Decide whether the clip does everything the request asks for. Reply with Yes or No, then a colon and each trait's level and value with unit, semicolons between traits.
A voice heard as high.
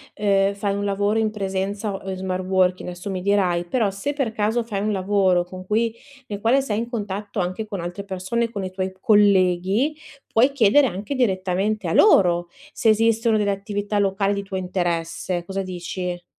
Yes: high, 200 Hz